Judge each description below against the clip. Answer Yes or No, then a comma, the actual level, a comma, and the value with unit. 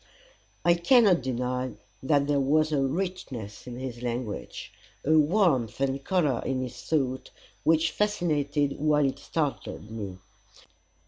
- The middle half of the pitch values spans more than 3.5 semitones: Yes, average, 3.9 semitones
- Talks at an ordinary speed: No, slow, 130 wpm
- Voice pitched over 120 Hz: Yes, medium, 140 Hz